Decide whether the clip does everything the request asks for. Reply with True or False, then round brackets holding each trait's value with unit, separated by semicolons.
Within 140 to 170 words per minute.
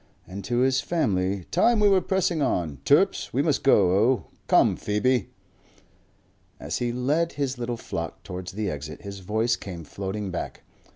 True (165 wpm)